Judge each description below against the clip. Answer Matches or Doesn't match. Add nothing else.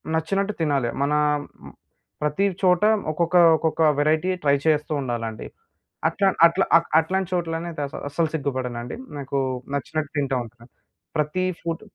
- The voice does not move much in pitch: Doesn't match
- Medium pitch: Matches